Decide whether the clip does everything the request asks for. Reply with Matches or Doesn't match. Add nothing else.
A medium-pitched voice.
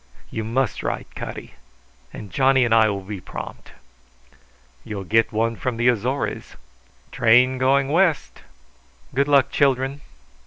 Doesn't match